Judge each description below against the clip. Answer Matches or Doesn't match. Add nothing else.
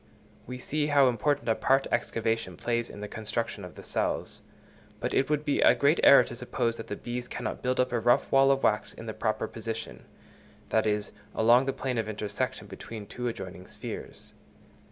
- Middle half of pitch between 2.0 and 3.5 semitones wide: Matches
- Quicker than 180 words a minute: Matches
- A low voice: Matches